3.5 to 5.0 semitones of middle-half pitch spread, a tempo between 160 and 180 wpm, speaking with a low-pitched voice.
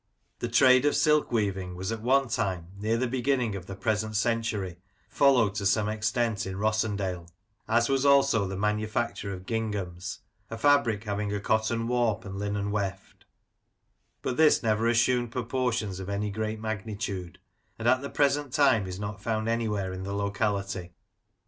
No: average, 3.0 semitones; average, 165 wpm; low, 110 Hz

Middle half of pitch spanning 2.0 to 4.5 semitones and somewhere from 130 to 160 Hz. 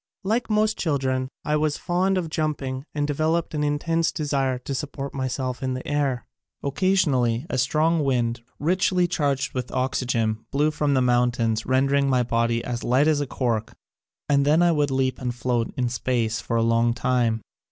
Yes: average, 3.6 semitones; low, 135 Hz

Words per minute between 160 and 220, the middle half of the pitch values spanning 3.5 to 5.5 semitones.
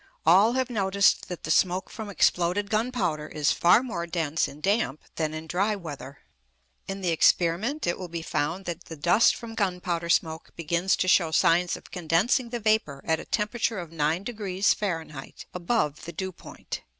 Yes: average, 175 wpm; average, 4.1 semitones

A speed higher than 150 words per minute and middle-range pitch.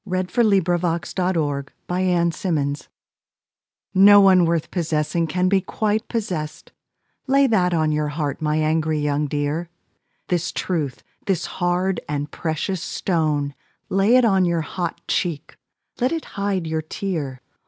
No: average, 145 wpm; medium, 175 Hz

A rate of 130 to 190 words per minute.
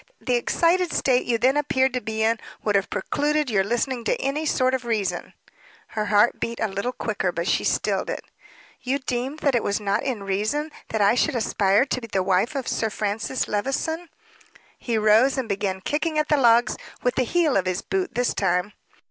No: fast, 205 wpm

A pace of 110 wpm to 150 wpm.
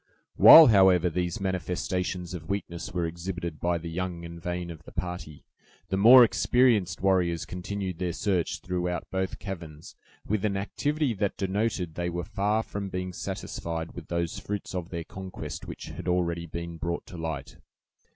No: average, 165 wpm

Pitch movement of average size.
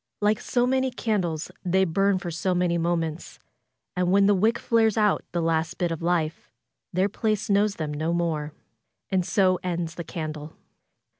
Yes: average, 3.4 semitones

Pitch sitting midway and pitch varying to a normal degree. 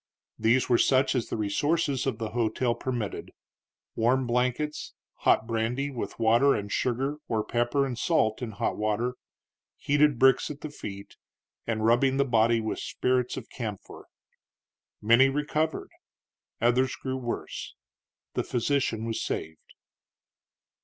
No: low, 120 Hz; average, 3.1 semitones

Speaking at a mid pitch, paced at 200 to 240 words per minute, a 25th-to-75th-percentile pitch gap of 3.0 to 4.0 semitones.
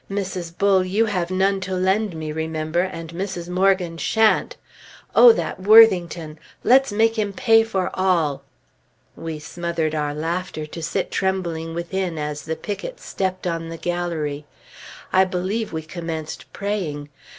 No: medium, 180 Hz; average, 145 wpm; average, 3.3 semitones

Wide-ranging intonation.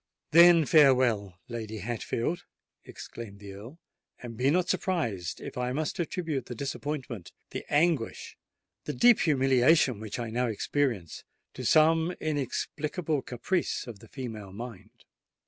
Yes: wide, 5.7 semitones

